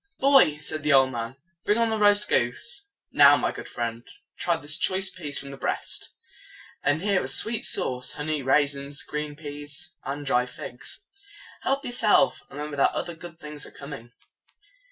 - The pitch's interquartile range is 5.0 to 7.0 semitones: Yes, average, 5.3 semitones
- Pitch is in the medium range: Yes, medium, 150 Hz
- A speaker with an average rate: Yes, average, 175 wpm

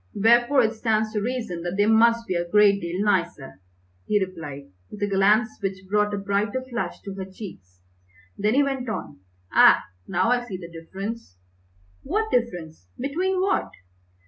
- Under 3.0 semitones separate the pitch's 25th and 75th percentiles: No, average, 4.0 semitones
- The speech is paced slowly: No, average, 170 wpm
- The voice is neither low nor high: No, high, 205 Hz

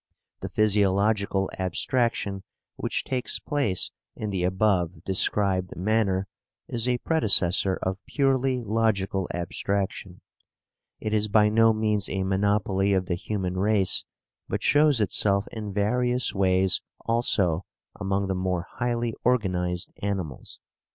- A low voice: Yes, low, 100 Hz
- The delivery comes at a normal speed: No, slow, 120 wpm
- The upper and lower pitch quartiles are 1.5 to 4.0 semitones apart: Yes, average, 2.9 semitones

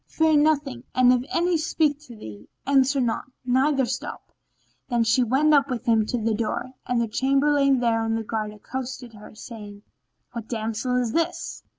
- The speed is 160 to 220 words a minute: Yes, average, 175 wpm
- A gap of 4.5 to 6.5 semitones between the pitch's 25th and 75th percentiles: No, average, 3.6 semitones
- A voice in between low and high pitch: No, very high, 250 Hz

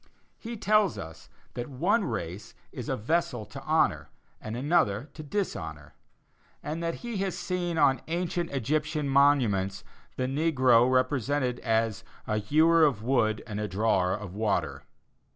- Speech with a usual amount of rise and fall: No, wide, 7.1 semitones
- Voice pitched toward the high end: No, low, 130 Hz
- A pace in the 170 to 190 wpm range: No, average, 145 wpm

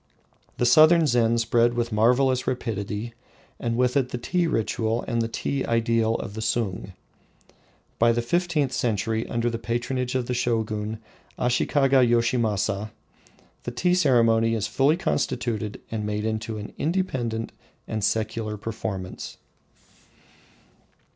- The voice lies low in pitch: Yes, low, 115 Hz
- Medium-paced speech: No, slow, 130 wpm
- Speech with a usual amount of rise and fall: No, narrow, 2.2 semitones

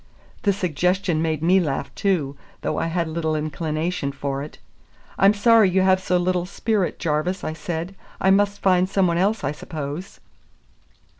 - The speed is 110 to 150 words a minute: No, average, 165 wpm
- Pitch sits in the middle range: Yes, medium, 175 Hz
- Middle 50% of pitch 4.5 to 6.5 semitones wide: No, average, 3.6 semitones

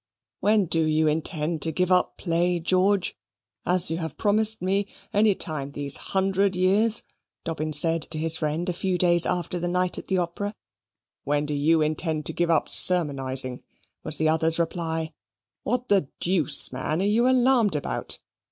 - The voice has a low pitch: No, medium, 170 Hz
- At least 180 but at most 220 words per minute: No, average, 170 wpm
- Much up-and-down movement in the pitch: No, average, 3.4 semitones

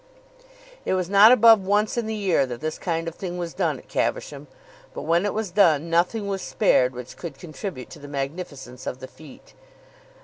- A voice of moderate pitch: Yes, medium, 175 Hz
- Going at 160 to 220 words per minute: Yes, average, 200 wpm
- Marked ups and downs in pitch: Yes, wide, 5.8 semitones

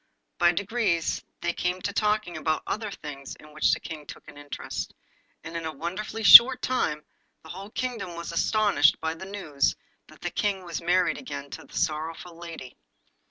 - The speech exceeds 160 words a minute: Yes, average, 180 wpm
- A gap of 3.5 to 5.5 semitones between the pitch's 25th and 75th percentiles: Yes, average, 4.5 semitones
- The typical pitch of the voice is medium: Yes, medium, 170 Hz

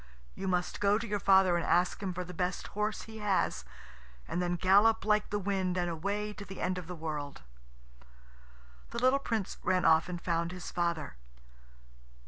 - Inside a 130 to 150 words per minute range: No, average, 185 wpm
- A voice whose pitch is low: No, medium, 185 Hz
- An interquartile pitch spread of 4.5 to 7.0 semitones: No, average, 2.9 semitones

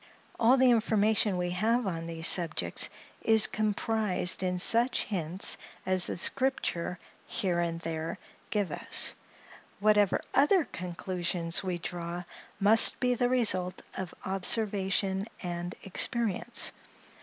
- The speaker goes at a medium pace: No, slow, 120 wpm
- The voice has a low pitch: No, high, 190 Hz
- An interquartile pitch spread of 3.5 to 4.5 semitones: Yes, average, 4.0 semitones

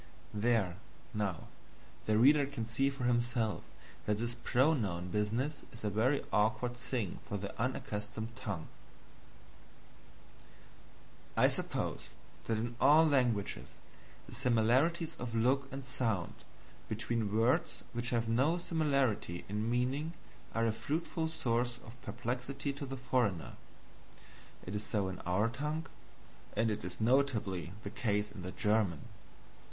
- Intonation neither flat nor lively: Yes, average, 4.0 semitones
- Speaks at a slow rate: Yes, slow, 130 wpm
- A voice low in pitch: Yes, low, 115 Hz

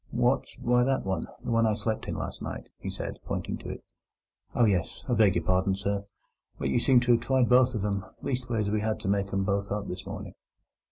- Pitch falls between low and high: No, low, 110 Hz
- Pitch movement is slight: No, average, 3.5 semitones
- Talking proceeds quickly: Yes, fast, 225 wpm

